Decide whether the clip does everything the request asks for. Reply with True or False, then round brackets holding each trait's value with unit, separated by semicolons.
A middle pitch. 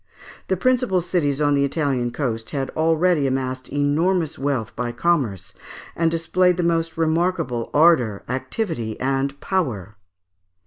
True (145 Hz)